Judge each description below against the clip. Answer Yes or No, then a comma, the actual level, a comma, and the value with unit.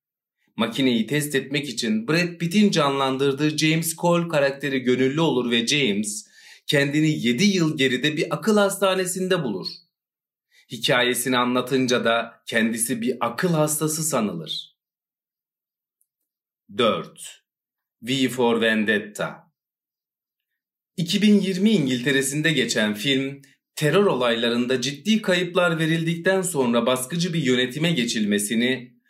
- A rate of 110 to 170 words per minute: No, average, 100 wpm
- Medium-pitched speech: Yes, medium, 145 Hz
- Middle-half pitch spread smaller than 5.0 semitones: No, wide, 5.5 semitones